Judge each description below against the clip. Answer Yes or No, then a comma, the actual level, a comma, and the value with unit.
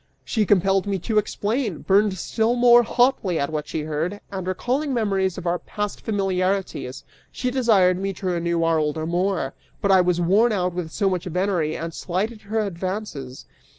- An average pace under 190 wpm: Yes, average, 180 wpm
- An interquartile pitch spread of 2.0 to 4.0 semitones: Yes, average, 3.6 semitones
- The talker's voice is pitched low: No, high, 190 Hz